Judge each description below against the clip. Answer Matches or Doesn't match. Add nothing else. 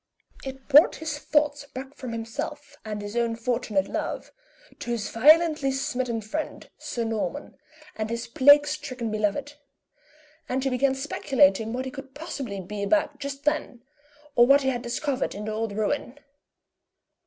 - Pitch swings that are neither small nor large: Matches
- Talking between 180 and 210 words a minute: Doesn't match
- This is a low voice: Doesn't match